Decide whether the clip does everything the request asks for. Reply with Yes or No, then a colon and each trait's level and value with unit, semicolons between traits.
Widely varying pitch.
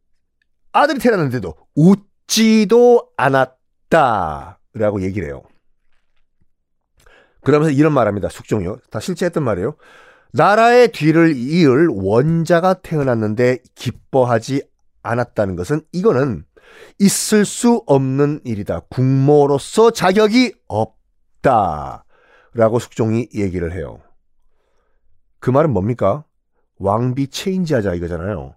Yes: wide, 8.3 semitones